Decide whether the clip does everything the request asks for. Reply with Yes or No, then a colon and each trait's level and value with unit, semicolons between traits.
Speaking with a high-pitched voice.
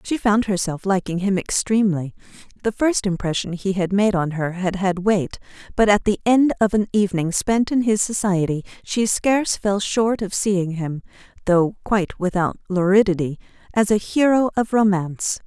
Yes: high, 195 Hz